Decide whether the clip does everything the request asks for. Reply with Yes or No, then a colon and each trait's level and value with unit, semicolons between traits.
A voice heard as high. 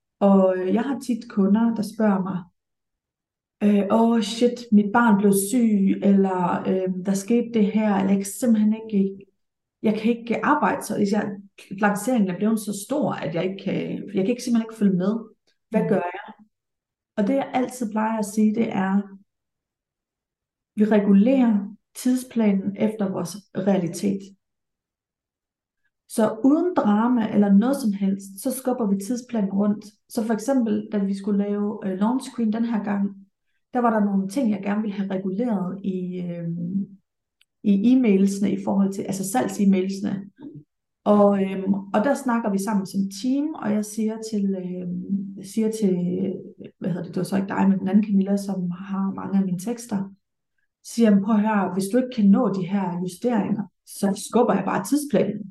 Yes: high, 205 Hz